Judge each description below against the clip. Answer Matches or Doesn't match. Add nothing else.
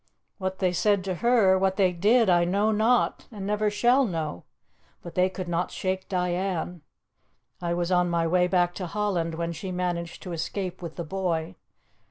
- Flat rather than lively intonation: Matches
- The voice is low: Doesn't match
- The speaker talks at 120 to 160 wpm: Doesn't match